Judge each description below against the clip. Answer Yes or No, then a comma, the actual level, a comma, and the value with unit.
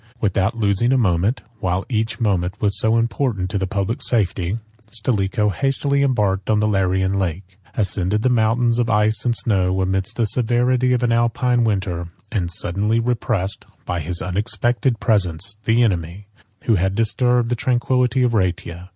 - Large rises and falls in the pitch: No, average, 4.0 semitones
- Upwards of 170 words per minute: No, average, 160 wpm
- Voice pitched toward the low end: Yes, low, 105 Hz